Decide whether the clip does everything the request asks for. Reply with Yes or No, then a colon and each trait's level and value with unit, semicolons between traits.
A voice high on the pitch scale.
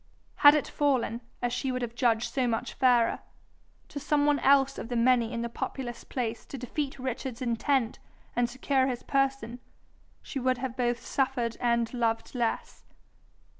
Yes: very high, 250 Hz